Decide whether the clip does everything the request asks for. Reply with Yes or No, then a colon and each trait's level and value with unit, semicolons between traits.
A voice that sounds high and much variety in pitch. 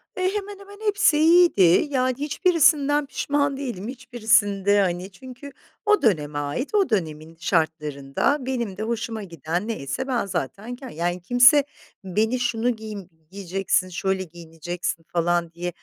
Yes: high, 215 Hz; wide, 7.4 semitones